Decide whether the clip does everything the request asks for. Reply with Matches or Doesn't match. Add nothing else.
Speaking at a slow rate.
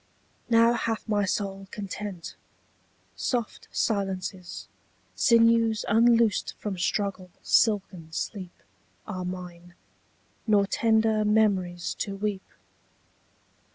Matches